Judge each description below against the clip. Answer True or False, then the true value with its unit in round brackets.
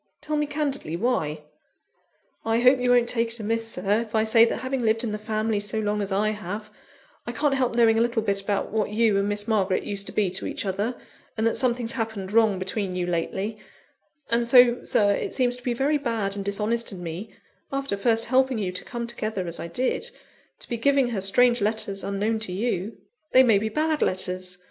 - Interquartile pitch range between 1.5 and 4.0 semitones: True (3.1 semitones)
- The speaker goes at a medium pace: False (215 wpm)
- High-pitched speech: True (220 Hz)